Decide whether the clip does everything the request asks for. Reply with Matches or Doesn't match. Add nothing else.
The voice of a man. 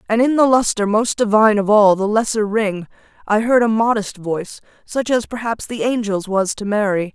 Doesn't match